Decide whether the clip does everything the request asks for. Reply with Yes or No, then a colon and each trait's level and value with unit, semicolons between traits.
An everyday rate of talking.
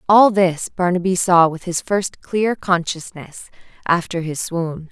Yes: average, 145 wpm